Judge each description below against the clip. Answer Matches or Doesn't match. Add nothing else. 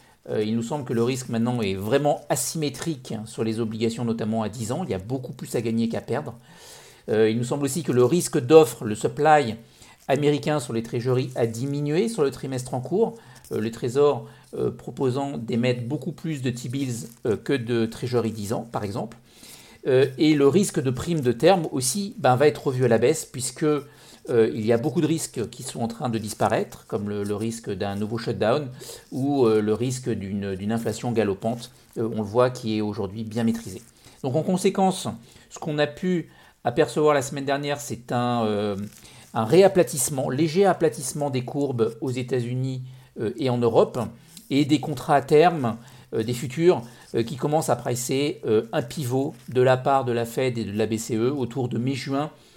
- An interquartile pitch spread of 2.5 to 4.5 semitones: Matches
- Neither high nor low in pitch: Doesn't match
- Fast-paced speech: Doesn't match